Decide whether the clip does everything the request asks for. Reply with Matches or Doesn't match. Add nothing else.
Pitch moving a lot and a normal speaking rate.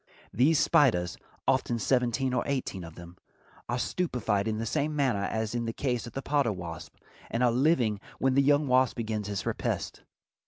Doesn't match